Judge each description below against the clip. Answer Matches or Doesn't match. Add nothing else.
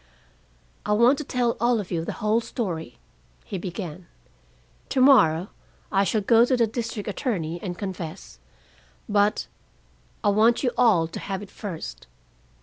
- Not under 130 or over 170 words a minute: Matches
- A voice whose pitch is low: Doesn't match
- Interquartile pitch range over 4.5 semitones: Matches